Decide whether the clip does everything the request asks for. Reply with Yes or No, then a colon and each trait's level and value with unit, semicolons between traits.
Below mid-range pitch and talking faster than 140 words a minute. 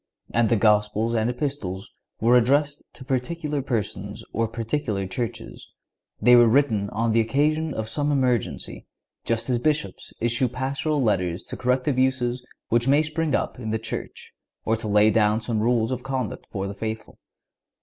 Yes: low, 120 Hz; average, 165 wpm